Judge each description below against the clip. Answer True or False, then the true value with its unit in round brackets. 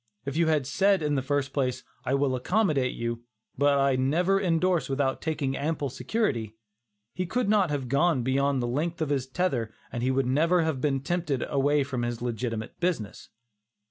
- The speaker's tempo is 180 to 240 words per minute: True (185 wpm)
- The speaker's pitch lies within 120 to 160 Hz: True (140 Hz)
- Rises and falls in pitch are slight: False (4.2 semitones)